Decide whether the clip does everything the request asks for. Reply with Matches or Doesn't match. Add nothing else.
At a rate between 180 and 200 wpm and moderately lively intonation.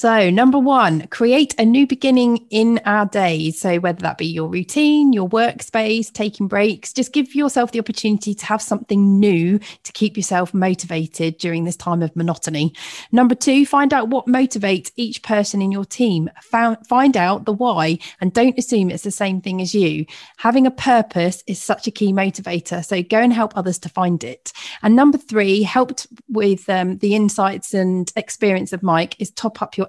Matches